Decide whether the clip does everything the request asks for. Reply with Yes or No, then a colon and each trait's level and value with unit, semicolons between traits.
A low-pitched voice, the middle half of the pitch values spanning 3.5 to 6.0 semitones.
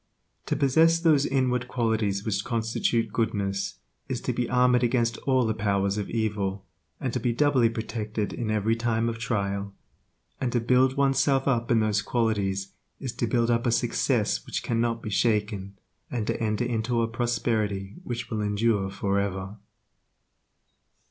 No: low, 115 Hz; average, 2.9 semitones